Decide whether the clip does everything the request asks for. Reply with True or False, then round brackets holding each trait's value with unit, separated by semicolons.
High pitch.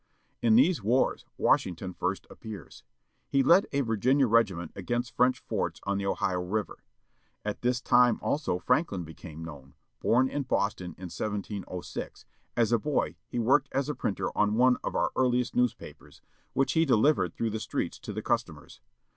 False (115 Hz)